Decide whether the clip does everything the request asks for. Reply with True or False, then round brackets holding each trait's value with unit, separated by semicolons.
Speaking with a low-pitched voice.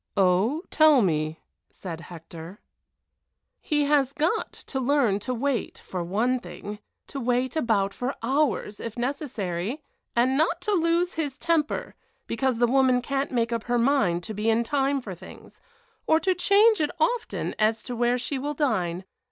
False (250 Hz)